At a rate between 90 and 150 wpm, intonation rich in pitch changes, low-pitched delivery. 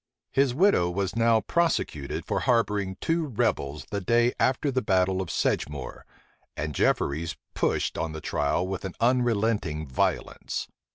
Yes: average, 145 wpm; wide, 6.7 semitones; low, 100 Hz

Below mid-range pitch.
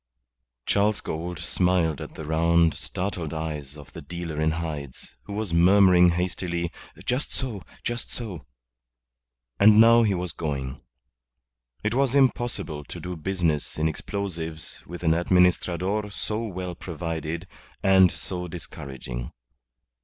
Yes: very low, 90 Hz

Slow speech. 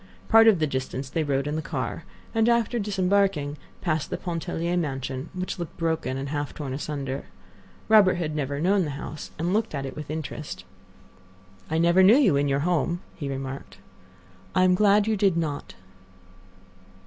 No: average, 175 wpm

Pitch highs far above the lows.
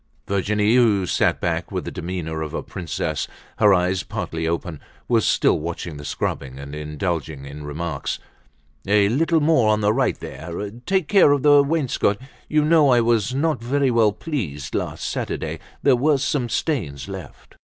Yes: wide, 8.9 semitones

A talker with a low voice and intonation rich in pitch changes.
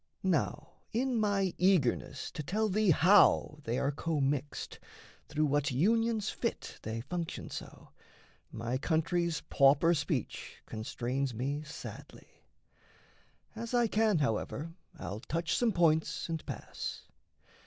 No: medium, 160 Hz; wide, 6.1 semitones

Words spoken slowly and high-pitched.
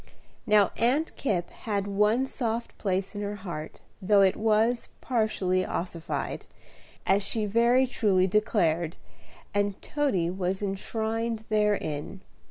Yes: slow, 120 wpm; high, 205 Hz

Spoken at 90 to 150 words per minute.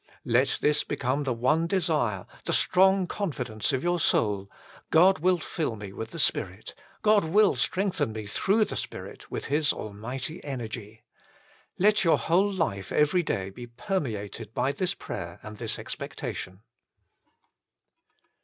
Yes: average, 145 wpm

